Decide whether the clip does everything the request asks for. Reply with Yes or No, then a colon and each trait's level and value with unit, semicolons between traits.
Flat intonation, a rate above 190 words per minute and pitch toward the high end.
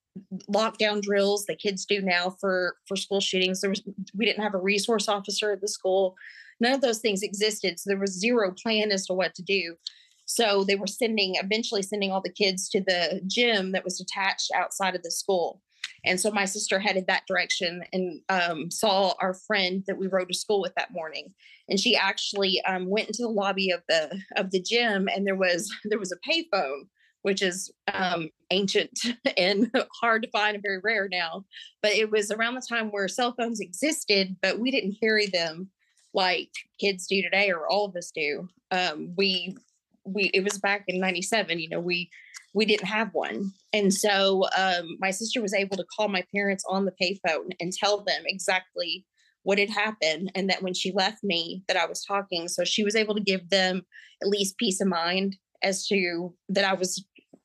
Yes: narrow, 2.0 semitones; fast, 205 wpm; high, 195 Hz